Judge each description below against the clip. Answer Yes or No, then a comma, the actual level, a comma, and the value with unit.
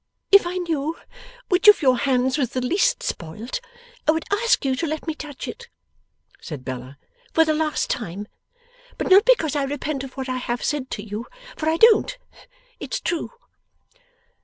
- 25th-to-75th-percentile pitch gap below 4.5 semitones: No, average, 5.2 semitones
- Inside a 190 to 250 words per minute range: No, average, 180 wpm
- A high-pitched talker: Yes, very high, 290 Hz